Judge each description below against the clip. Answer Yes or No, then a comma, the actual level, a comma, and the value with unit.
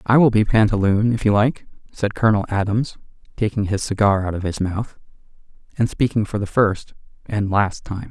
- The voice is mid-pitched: No, low, 105 Hz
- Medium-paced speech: Yes, average, 185 wpm